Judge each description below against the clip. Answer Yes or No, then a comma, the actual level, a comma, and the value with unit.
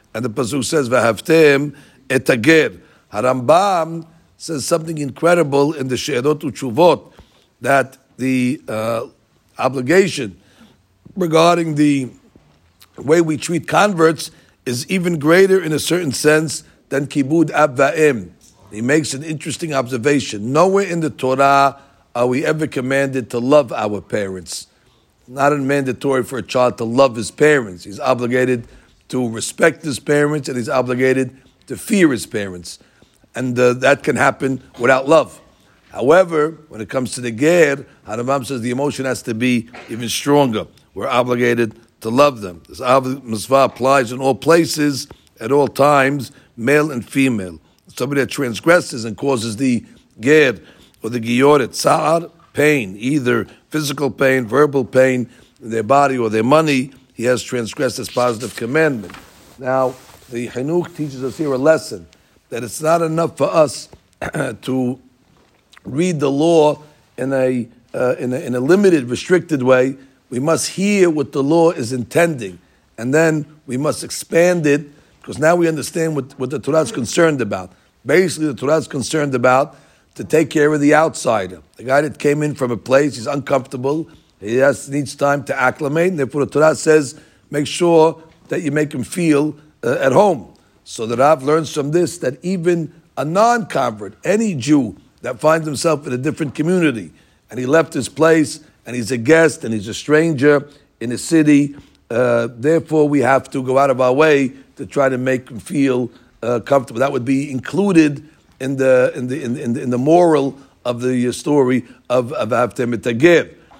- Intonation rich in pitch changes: No, average, 3.7 semitones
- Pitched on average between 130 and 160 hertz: Yes, low, 135 Hz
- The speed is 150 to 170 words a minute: Yes, average, 165 wpm